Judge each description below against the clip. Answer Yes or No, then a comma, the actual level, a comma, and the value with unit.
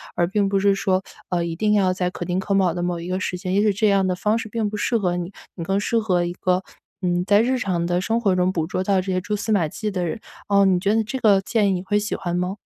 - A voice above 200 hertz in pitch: No, high, 190 Hz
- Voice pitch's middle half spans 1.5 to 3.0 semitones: Yes, narrow, 2.5 semitones